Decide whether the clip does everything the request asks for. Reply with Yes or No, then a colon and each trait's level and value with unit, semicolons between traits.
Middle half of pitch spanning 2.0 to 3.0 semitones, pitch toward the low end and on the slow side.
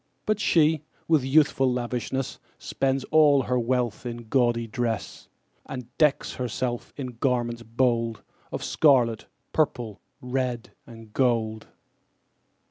Yes: narrow, 2.4 semitones; low, 125 Hz; slow, 115 wpm